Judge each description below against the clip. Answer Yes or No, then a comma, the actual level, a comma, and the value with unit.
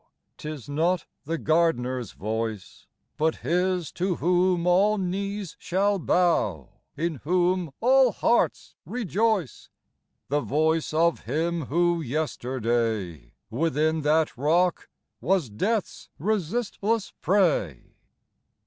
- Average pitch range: Yes, average, 4.6 semitones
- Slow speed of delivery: Yes, slow, 105 wpm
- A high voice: No, medium, 165 Hz